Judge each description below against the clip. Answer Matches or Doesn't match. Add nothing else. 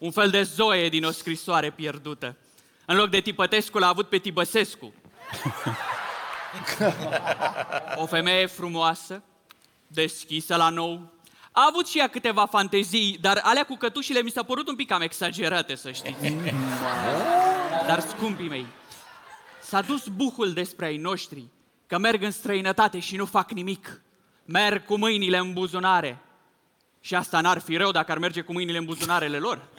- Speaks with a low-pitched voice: Doesn't match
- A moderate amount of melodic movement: Matches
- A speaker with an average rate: Matches